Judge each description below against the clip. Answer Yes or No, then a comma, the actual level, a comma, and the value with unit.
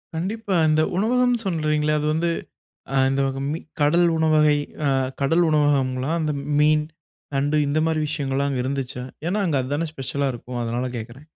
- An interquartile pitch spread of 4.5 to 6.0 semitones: No, average, 2.9 semitones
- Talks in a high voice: No, medium, 150 Hz